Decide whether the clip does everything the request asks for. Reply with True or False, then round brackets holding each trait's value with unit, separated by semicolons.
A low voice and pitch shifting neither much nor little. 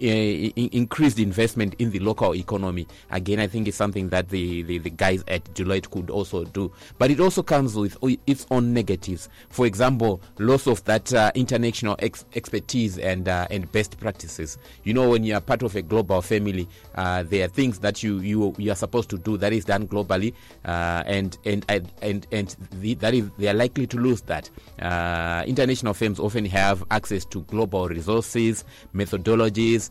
True (105 Hz; 3.2 semitones)